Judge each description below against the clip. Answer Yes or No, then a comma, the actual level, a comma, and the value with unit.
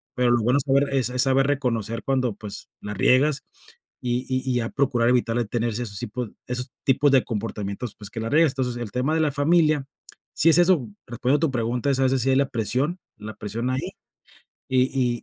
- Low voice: Yes, low, 125 Hz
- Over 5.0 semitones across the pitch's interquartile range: No, average, 2.8 semitones